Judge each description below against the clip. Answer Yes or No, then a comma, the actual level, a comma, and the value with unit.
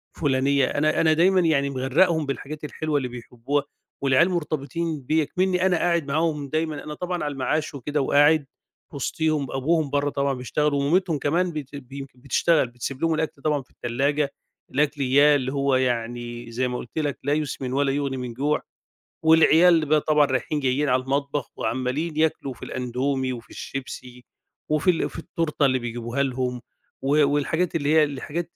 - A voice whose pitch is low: No, medium, 145 Hz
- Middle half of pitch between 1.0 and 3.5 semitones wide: Yes, average, 3.0 semitones